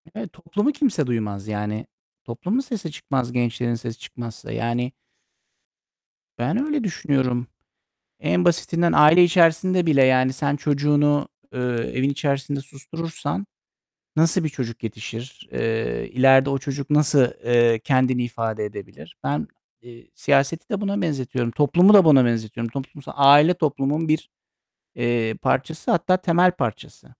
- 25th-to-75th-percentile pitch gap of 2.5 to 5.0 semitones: No, wide, 5.4 semitones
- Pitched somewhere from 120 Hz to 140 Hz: Yes, low, 135 Hz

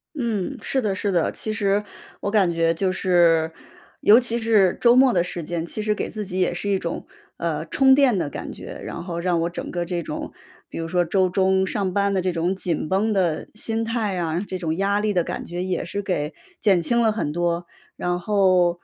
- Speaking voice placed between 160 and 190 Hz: Yes, medium, 185 Hz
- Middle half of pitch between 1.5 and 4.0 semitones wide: Yes, average, 3.3 semitones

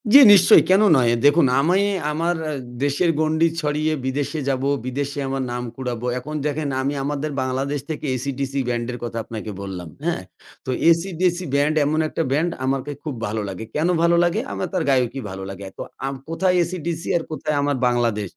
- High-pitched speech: No, medium, 140 Hz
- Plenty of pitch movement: No, average, 4.1 semitones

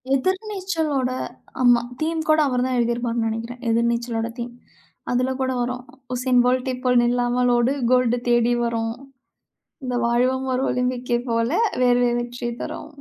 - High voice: Yes, high, 245 Hz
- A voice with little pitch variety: Yes, narrow, 1.3 semitones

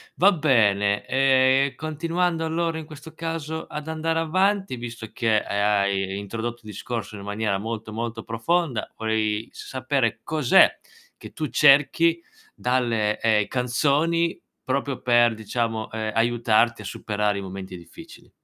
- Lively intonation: Yes, wide, 6.2 semitones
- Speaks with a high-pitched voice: No, low, 120 Hz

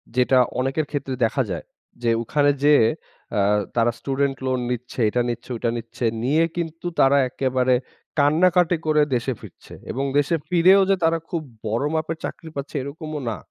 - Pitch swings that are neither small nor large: Yes, average, 4.1 semitones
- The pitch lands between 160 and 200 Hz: No, medium, 140 Hz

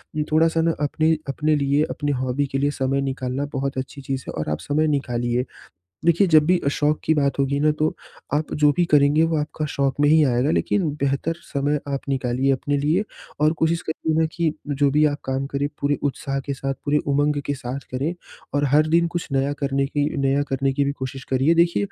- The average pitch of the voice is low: No, medium, 145 Hz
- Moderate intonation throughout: No, narrow, 2.0 semitones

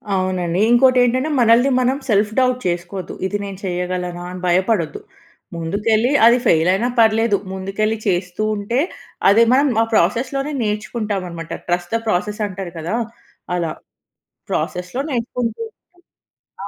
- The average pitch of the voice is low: No, high, 205 Hz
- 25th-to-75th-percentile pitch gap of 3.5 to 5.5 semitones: Yes, average, 4.6 semitones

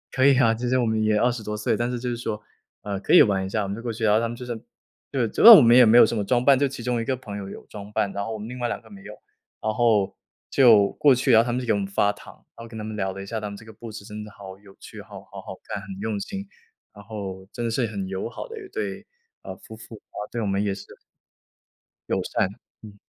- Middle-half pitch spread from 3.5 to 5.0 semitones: No, average, 2.9 semitones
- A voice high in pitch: No, low, 110 Hz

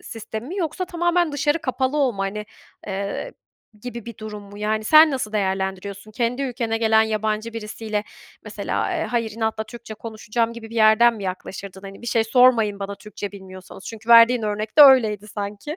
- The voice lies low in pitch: No, high, 220 Hz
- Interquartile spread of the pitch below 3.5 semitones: Yes, average, 2.7 semitones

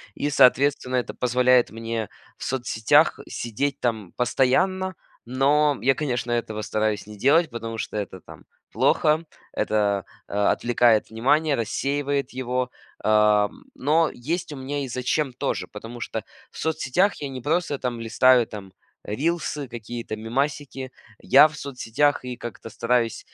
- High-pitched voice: No, low, 125 Hz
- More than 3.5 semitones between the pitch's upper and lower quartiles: Yes, average, 4.0 semitones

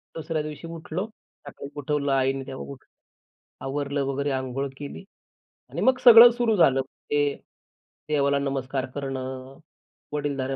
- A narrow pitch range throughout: Yes, narrow, 1.9 semitones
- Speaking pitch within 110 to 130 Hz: No, medium, 140 Hz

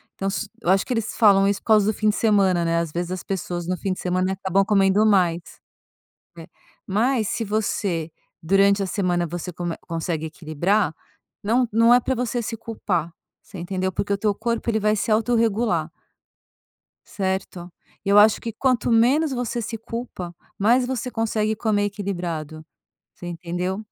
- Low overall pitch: No, high, 200 Hz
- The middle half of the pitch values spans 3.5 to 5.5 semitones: Yes, average, 4.1 semitones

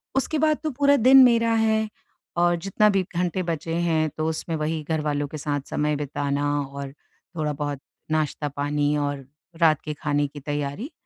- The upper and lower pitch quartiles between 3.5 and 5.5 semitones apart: Yes, average, 5.0 semitones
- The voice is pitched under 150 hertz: No, medium, 155 Hz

